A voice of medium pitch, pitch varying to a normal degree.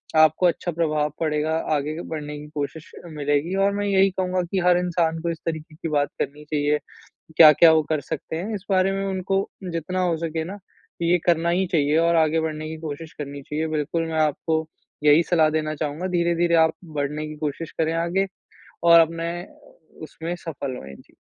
No: medium, 160 Hz; narrow, 2.2 semitones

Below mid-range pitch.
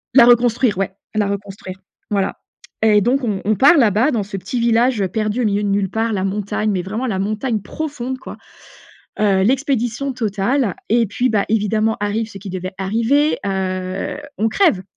No: high, 215 Hz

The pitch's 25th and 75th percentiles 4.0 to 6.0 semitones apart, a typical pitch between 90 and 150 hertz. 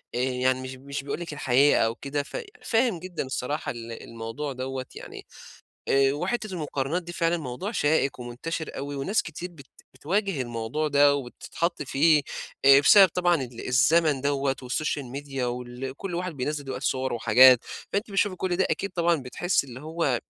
Yes: average, 4.7 semitones; medium, 140 Hz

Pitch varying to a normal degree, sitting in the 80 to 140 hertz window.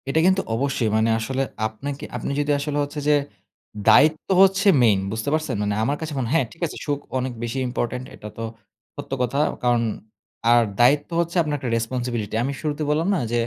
Yes: average, 4.0 semitones; low, 135 Hz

